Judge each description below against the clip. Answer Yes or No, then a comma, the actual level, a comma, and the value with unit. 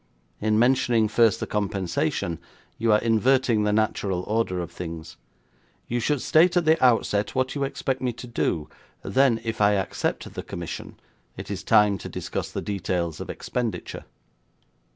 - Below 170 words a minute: Yes, average, 160 wpm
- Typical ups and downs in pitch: Yes, average, 3.8 semitones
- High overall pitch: No, low, 110 Hz